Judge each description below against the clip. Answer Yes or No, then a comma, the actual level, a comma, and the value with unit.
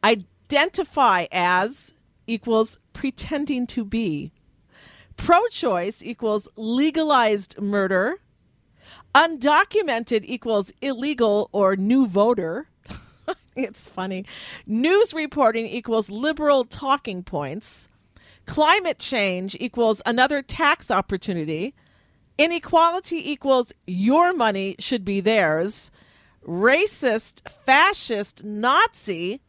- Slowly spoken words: Yes, slow, 85 wpm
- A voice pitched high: Yes, high, 230 Hz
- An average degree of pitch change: No, wide, 6.3 semitones